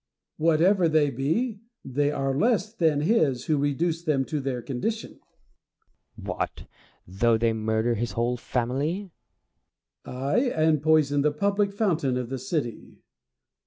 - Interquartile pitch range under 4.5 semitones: No, average, 5.1 semitones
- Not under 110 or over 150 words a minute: Yes, average, 140 wpm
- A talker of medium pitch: Yes, medium, 145 Hz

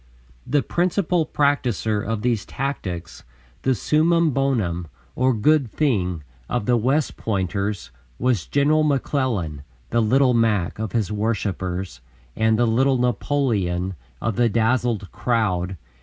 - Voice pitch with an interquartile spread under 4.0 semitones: No, wide, 5.5 semitones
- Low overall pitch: Yes, low, 115 Hz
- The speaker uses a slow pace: Yes, slow, 125 wpm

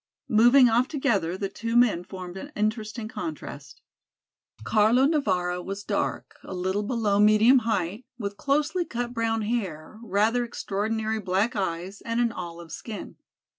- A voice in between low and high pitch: No, high, 215 Hz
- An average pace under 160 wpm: Yes, average, 140 wpm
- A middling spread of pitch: Yes, average, 3.9 semitones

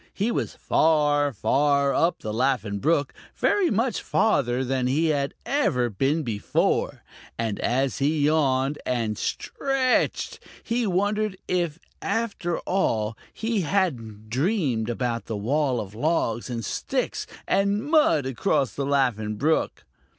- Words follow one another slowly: Yes, slow, 130 wpm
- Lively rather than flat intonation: Yes, wide, 7.2 semitones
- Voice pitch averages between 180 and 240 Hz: No, medium, 140 Hz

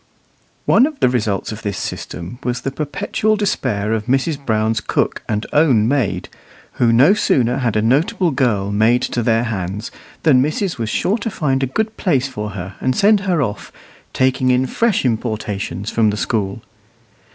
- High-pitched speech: No, low, 125 Hz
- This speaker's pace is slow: No, average, 175 wpm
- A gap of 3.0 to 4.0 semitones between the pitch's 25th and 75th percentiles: No, average, 5.1 semitones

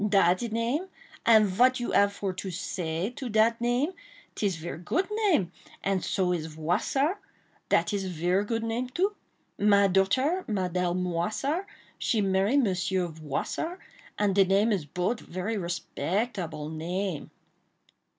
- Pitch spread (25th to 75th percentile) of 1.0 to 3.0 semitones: No, average, 4.9 semitones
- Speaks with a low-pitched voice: No, high, 200 Hz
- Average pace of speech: No, slow, 130 wpm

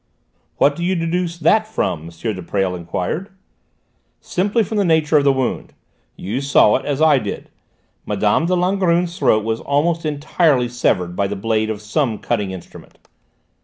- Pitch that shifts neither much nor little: No, wide, 8.4 semitones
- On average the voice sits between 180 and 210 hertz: No, medium, 140 Hz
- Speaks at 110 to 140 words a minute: No, average, 165 wpm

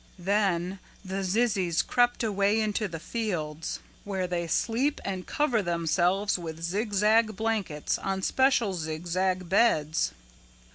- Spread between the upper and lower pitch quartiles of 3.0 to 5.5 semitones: Yes, average, 3.9 semitones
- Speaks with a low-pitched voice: No, high, 195 Hz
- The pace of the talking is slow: Yes, slow, 115 wpm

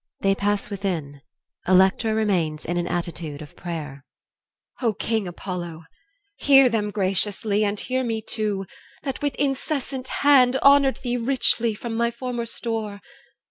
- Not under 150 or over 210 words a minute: No, average, 140 wpm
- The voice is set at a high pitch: Yes, high, 210 Hz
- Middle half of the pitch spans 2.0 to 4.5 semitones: No, average, 5.2 semitones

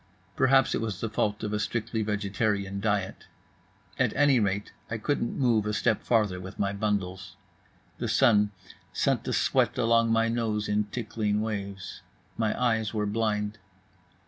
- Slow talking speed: No, average, 155 wpm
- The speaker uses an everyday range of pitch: No, narrow, 1.8 semitones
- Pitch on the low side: Yes, low, 105 Hz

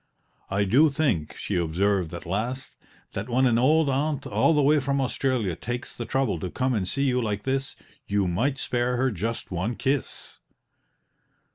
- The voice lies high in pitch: No, low, 125 Hz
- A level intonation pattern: No, average, 5.2 semitones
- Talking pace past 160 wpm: Yes, average, 175 wpm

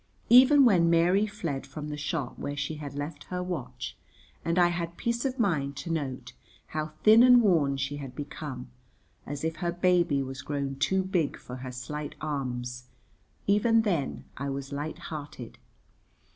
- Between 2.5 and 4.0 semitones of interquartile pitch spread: No, average, 4.7 semitones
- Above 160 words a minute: Yes, average, 170 wpm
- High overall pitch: No, medium, 150 Hz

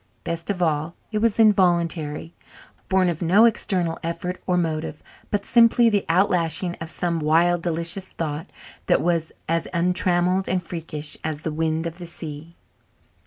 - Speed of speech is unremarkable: Yes, average, 155 wpm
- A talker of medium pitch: Yes, medium, 170 Hz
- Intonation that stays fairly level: Yes, narrow, 2.2 semitones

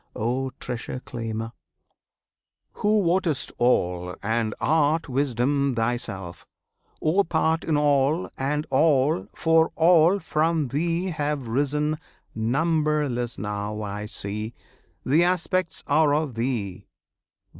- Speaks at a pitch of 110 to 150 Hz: Yes, medium, 140 Hz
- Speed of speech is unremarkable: No, slow, 105 wpm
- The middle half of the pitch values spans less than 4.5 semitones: No, wide, 5.5 semitones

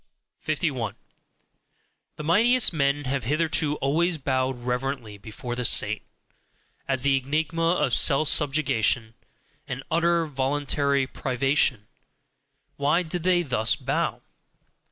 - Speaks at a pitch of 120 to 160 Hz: Yes, medium, 140 Hz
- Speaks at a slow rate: Yes, slow, 110 wpm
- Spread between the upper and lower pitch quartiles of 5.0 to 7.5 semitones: No, average, 3.5 semitones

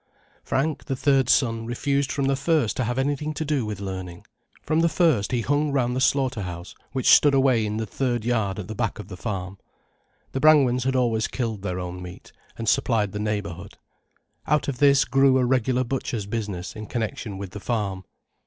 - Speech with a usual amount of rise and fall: Yes, average, 4.7 semitones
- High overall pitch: No, low, 120 Hz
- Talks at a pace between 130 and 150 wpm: No, average, 200 wpm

